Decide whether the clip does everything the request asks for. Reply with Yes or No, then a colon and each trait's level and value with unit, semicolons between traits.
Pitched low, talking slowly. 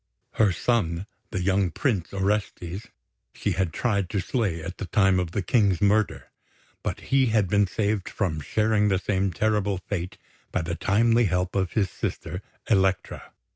No: very low, 95 Hz; average, 165 wpm